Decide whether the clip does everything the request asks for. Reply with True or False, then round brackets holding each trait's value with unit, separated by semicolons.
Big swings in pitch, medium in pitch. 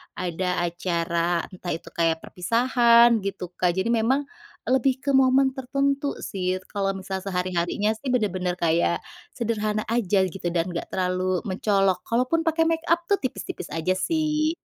False (6.1 semitones; 195 Hz)